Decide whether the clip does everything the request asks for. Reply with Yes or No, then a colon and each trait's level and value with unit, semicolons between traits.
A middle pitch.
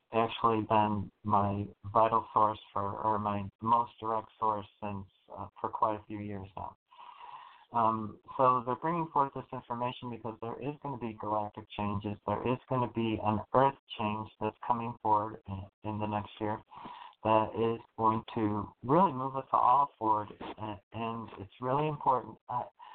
No: low, 110 Hz